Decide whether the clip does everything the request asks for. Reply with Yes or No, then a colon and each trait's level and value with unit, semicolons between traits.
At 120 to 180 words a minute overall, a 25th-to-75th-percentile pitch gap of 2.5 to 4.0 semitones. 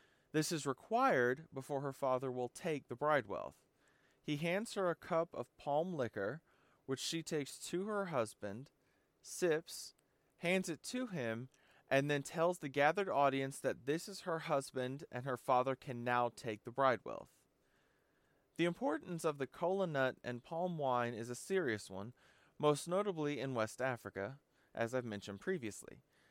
No: average, 160 wpm; average, 4.6 semitones